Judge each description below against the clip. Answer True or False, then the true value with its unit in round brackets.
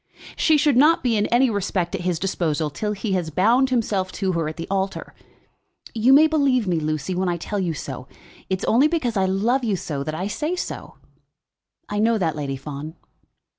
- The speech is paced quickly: True (210 wpm)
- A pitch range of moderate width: False (6.3 semitones)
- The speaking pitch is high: True (195 Hz)